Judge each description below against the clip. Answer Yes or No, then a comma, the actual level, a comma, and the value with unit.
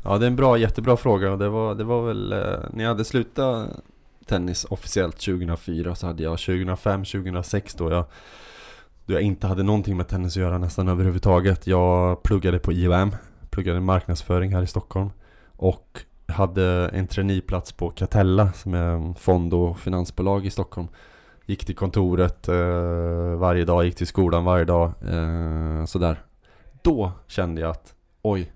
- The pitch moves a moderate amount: No, narrow, 2.2 semitones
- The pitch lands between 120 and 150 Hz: No, very low, 90 Hz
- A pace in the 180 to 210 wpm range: No, average, 165 wpm